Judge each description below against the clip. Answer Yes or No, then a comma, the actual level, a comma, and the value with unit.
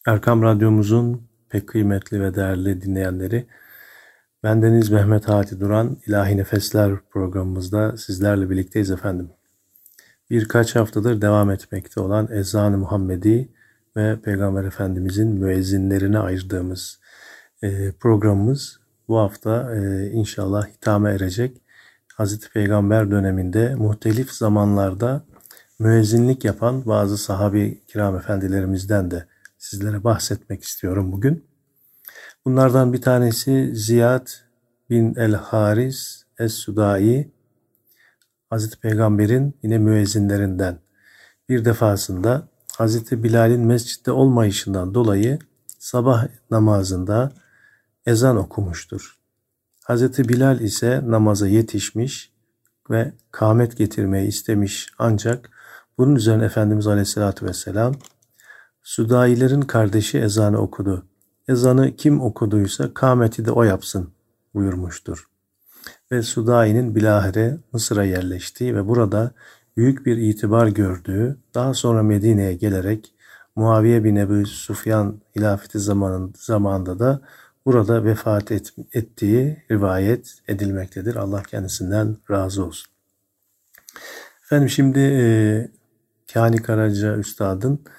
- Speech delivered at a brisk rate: No, slow, 95 wpm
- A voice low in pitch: Yes, low, 110 Hz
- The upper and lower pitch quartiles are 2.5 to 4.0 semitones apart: Yes, average, 2.9 semitones